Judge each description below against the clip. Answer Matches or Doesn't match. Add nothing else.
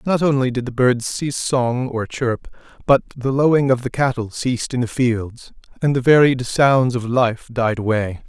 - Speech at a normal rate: Matches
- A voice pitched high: Doesn't match